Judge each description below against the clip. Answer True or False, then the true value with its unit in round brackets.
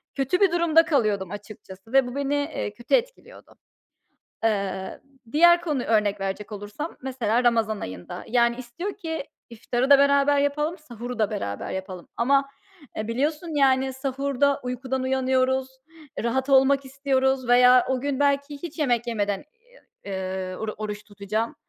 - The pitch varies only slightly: False (4.6 semitones)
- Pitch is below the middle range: False (255 Hz)